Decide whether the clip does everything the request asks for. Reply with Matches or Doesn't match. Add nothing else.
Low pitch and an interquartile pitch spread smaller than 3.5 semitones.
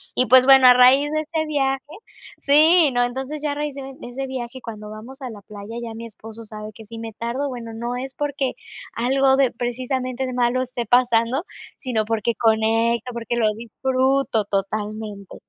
Doesn't match